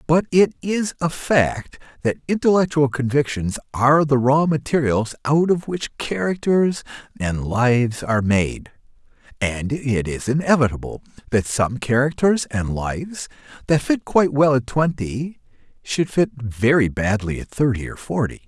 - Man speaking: Yes, male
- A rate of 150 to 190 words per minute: No, average, 140 wpm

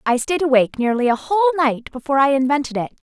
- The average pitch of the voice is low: No, very high, 275 Hz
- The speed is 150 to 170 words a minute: No, fast, 205 wpm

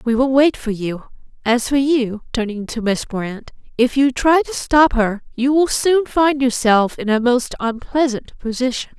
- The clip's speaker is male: No, female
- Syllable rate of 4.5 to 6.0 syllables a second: No, 4.3 syllables/s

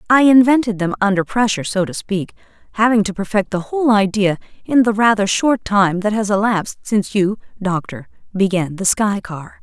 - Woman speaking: Yes, female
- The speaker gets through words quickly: No, average, 180 wpm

